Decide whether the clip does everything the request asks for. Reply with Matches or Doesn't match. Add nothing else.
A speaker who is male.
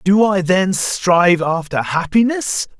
Matches